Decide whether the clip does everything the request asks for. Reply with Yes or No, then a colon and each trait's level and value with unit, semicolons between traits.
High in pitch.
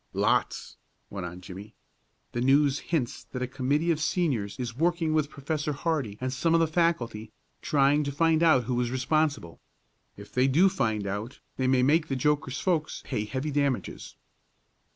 No: medium, 140 Hz